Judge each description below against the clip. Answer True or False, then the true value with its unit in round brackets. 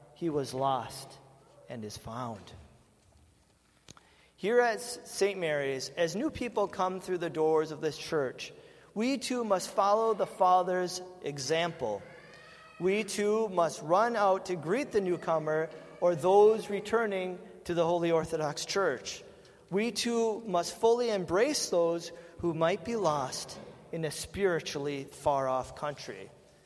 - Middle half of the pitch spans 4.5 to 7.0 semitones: True (5.2 semitones)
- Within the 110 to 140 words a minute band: True (135 wpm)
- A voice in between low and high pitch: True (170 Hz)